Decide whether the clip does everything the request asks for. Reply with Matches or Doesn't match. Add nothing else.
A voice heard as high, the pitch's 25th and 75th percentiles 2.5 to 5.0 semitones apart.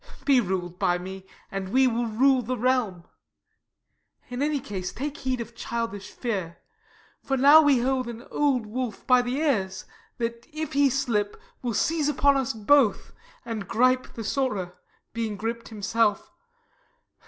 Matches